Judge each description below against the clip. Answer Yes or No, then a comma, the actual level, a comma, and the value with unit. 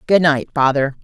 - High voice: No, medium, 150 Hz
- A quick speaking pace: No, average, 175 wpm